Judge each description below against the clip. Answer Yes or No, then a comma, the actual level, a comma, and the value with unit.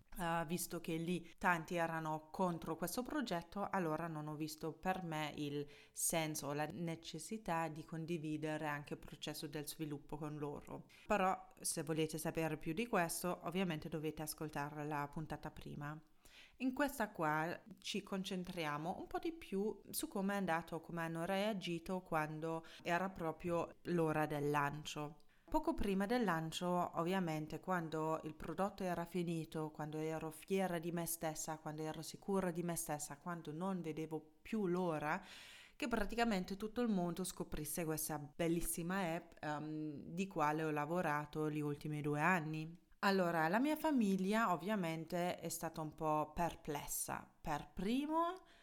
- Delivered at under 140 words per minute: No, average, 150 wpm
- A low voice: No, medium, 165 Hz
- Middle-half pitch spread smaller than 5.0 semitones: Yes, average, 3.2 semitones